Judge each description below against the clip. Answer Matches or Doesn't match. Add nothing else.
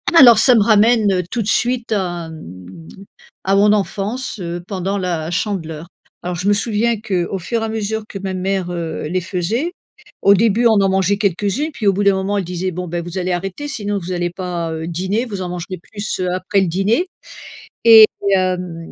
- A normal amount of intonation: Matches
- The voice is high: Matches